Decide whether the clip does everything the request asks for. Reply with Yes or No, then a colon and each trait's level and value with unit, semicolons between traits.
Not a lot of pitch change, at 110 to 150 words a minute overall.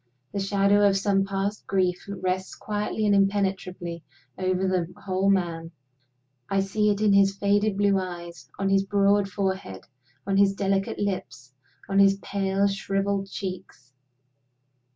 Yes: narrow, 1.2 semitones; average, 140 wpm